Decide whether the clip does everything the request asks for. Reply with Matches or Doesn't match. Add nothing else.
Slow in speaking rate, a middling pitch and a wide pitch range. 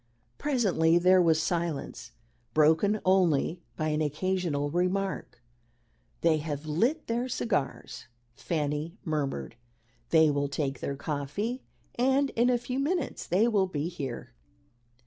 Matches